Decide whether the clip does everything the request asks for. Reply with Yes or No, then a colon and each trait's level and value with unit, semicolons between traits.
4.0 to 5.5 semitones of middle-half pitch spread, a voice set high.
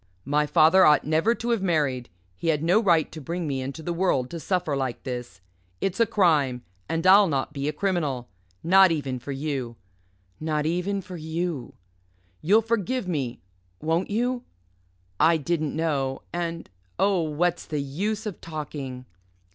No: average, 4.8 semitones; medium, 160 Hz